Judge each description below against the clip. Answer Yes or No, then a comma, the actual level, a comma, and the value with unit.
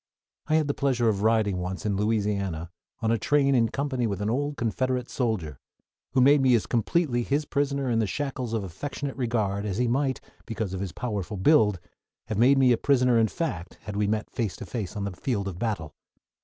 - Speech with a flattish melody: No, average, 4.6 semitones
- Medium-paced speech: No, fast, 210 wpm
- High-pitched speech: No, low, 115 Hz